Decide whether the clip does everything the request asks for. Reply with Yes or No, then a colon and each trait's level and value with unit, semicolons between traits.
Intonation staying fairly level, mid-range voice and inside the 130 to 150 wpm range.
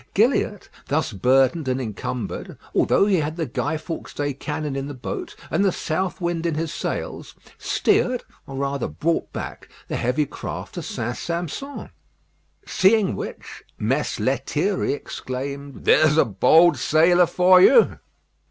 No: average, 4.6 semitones; medium, 155 Hz; average, 145 wpm